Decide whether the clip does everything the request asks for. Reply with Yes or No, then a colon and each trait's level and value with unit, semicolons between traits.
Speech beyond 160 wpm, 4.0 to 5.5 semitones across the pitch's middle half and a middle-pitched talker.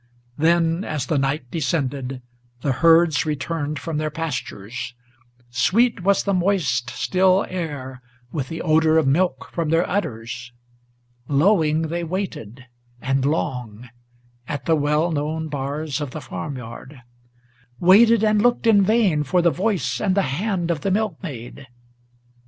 No: average, 140 wpm; average, 5.0 semitones; medium, 155 Hz